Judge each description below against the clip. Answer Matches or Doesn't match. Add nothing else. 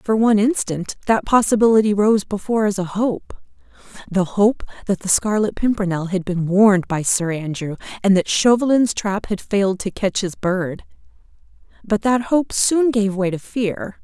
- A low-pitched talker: Doesn't match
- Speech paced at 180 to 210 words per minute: Doesn't match